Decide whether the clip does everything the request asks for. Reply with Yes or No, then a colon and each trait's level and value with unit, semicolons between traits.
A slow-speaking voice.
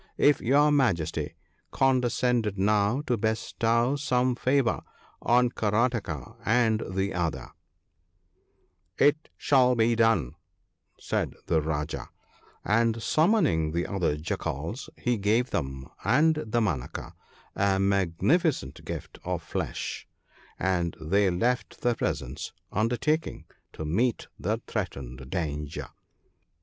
Yes: slow, 115 wpm